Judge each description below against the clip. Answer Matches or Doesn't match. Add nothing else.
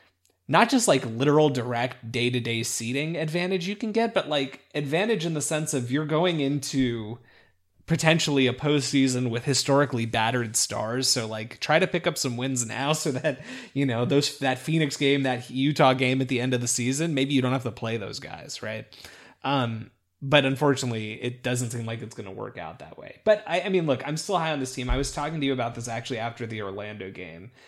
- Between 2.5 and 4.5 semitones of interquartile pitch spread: Matches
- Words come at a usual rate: Doesn't match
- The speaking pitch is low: Matches